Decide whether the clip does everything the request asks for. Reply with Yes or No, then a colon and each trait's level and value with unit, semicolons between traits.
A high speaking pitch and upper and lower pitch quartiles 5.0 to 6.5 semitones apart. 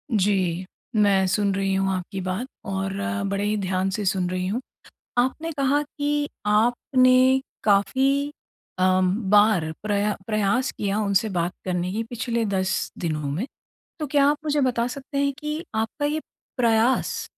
Yes: high, 210 Hz; wide, 5.5 semitones